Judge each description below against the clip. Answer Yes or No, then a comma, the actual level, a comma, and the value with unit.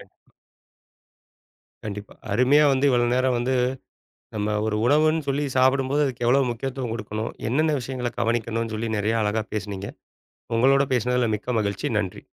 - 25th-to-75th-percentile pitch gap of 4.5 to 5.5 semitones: No, average, 3.4 semitones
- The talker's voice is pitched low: Yes, low, 120 Hz